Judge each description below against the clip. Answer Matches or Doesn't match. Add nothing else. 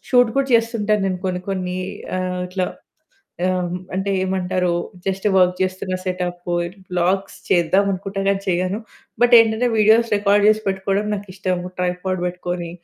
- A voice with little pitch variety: Matches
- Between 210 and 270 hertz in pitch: Doesn't match